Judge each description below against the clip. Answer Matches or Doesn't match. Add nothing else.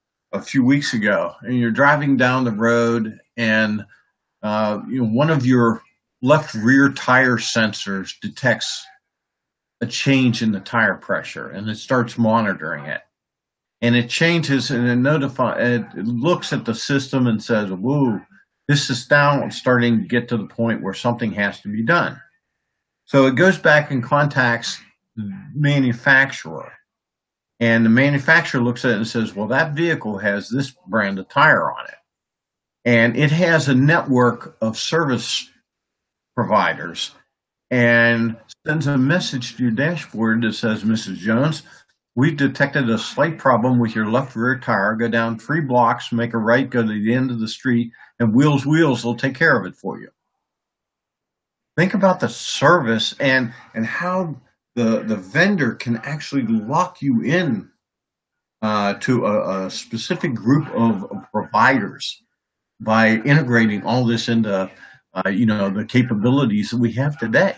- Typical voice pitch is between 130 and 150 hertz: Doesn't match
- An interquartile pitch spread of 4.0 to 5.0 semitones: Doesn't match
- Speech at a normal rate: Matches